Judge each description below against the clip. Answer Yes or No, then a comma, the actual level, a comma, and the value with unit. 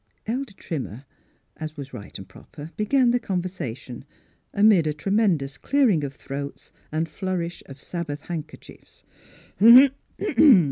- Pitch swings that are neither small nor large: No, wide, 5.8 semitones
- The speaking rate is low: Yes, slow, 125 wpm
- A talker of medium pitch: Yes, medium, 160 Hz